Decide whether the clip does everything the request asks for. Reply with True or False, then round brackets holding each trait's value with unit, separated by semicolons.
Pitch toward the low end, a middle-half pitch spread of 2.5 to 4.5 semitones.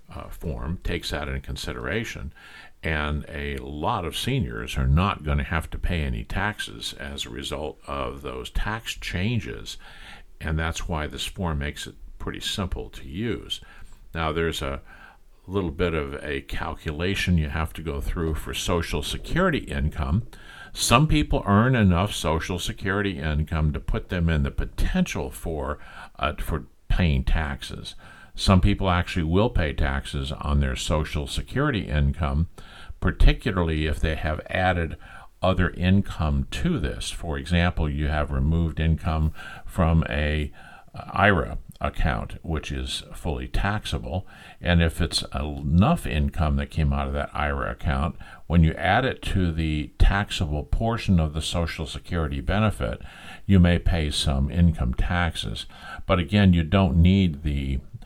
True (80 Hz; 3.7 semitones)